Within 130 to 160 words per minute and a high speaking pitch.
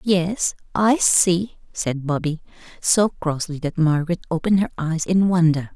No: average, 145 wpm; medium, 170 Hz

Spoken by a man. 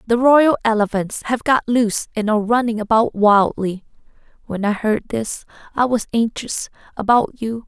No: female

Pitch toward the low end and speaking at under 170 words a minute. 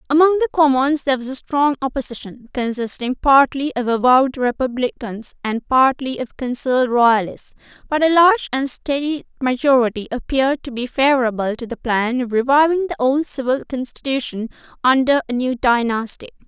No: very high, 260 Hz; average, 150 wpm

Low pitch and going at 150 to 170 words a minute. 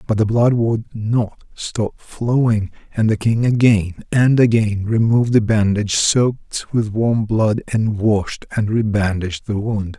Yes: low, 110 Hz; average, 155 wpm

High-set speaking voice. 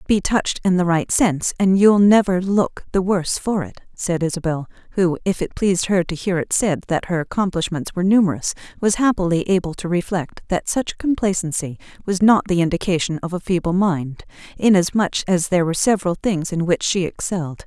No: medium, 180 Hz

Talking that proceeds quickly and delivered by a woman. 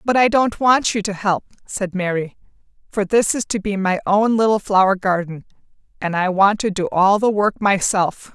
Yes: fast, 210 wpm; female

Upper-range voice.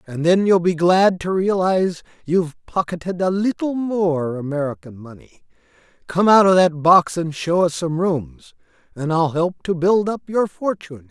No: medium, 175 Hz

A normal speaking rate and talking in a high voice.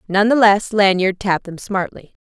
Yes: average, 190 wpm; high, 200 Hz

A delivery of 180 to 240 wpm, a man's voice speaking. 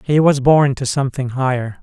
Yes: average, 200 wpm; male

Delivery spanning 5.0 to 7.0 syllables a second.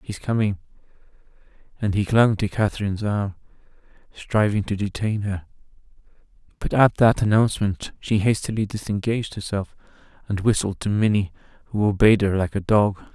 Yes: 5.4 syllables/s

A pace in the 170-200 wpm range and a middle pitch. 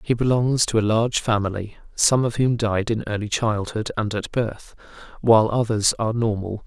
No: average, 180 wpm; low, 110 Hz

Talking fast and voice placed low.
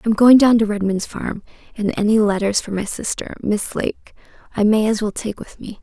No: fast, 215 wpm; high, 215 Hz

